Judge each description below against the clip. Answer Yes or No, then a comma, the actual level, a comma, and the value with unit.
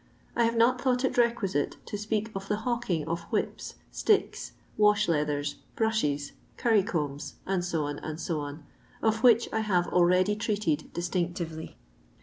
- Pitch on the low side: No, high, 195 Hz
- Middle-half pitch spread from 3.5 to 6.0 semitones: Yes, average, 5.3 semitones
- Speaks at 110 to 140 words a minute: Yes, slow, 135 wpm